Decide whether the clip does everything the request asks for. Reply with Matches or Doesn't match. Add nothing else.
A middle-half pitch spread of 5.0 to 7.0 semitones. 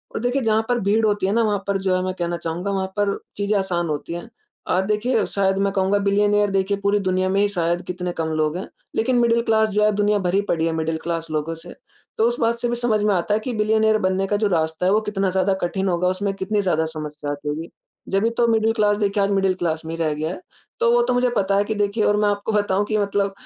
Doesn't match